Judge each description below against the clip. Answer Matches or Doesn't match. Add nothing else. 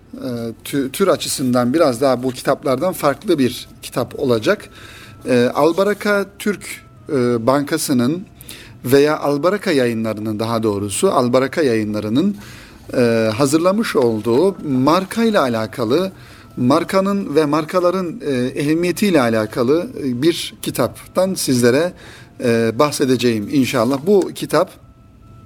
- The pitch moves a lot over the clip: Matches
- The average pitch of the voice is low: Matches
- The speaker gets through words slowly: Matches